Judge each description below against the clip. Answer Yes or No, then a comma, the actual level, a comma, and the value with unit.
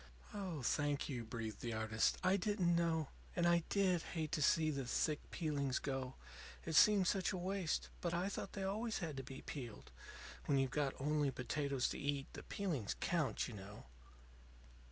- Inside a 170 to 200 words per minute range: Yes, average, 180 wpm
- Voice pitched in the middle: Yes, medium, 150 Hz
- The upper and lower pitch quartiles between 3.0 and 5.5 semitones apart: Yes, average, 4.9 semitones